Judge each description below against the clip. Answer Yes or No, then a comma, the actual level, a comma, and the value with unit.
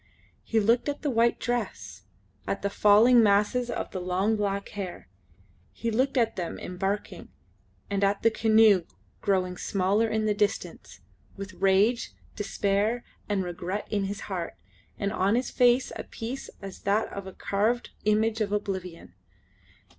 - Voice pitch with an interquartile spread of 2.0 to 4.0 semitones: Yes, narrow, 2.6 semitones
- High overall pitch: Yes, high, 205 Hz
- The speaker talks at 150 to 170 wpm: Yes, average, 155 wpm